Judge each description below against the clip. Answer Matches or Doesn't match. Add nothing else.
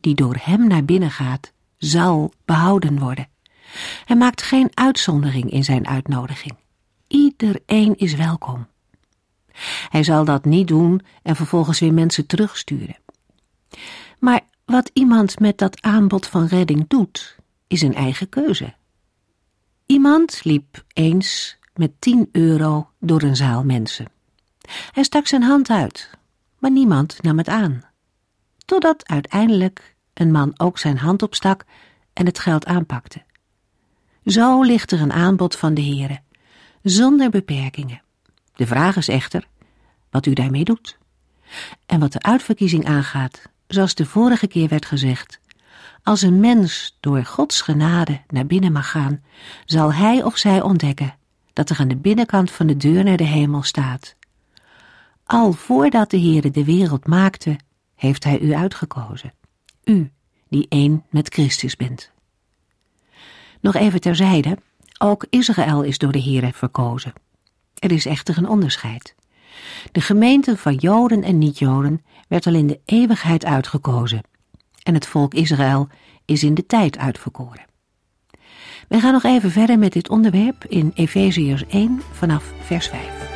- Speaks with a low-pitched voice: Doesn't match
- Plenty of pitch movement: Matches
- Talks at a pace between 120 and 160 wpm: Matches